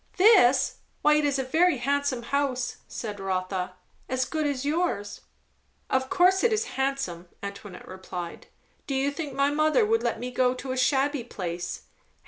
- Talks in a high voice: Yes, very high, 265 Hz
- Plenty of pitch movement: Yes, wide, 6.0 semitones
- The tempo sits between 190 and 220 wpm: No, average, 165 wpm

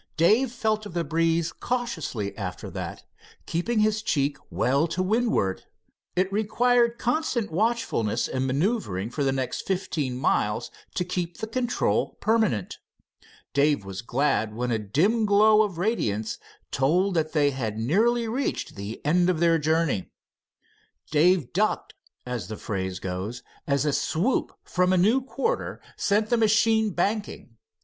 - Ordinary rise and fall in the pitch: No, wide, 8.8 semitones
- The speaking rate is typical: Yes, average, 145 wpm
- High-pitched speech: No, medium, 170 Hz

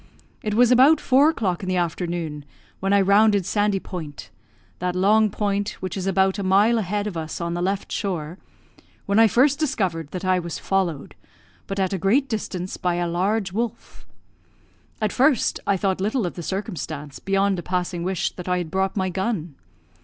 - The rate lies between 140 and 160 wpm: No, average, 190 wpm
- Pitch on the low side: No, high, 190 Hz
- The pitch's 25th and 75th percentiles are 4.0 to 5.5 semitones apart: No, average, 2.9 semitones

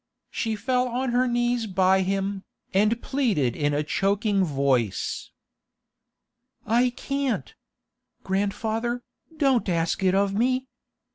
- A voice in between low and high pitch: No, high, 210 Hz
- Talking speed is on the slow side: Yes, slow, 115 wpm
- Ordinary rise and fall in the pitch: Yes, average, 4.4 semitones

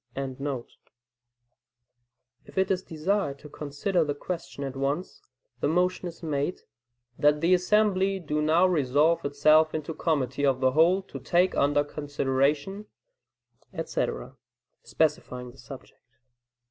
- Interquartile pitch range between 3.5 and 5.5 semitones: Yes, average, 4.7 semitones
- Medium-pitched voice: Yes, medium, 145 Hz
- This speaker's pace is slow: Yes, slow, 130 wpm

